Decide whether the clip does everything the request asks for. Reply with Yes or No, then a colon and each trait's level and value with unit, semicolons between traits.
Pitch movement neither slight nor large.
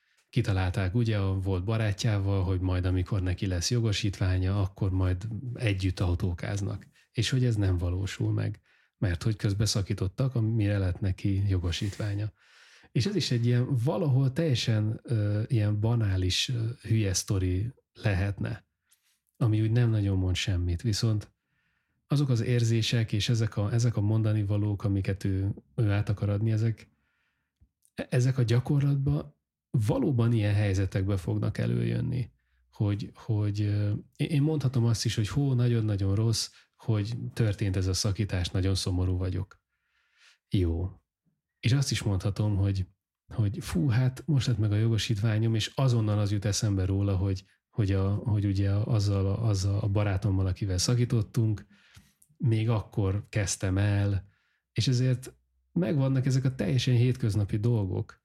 Yes: average, 3.1 semitones